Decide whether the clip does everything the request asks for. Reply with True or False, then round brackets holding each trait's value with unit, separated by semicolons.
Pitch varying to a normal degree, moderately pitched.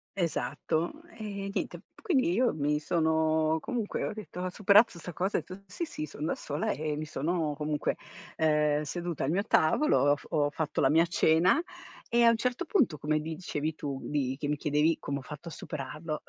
True (4.0 semitones; 160 Hz)